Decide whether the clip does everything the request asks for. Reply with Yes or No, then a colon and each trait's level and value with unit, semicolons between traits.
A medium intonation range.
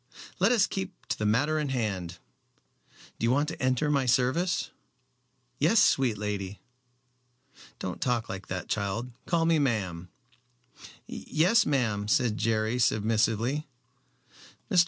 No: wide, 5.9 semitones